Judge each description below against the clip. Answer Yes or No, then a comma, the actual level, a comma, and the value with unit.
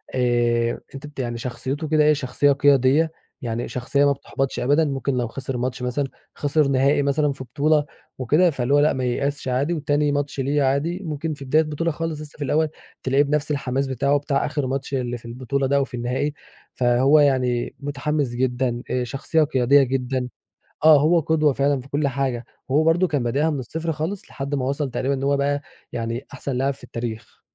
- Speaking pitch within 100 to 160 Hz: Yes, medium, 140 Hz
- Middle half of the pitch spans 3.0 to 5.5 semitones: No, narrow, 2.5 semitones